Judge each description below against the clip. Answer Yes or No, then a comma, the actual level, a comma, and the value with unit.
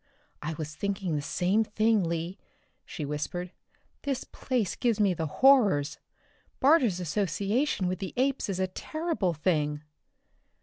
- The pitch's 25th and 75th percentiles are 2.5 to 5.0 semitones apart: No, wide, 5.5 semitones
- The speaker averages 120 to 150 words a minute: Yes, average, 140 wpm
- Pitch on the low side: No, high, 190 Hz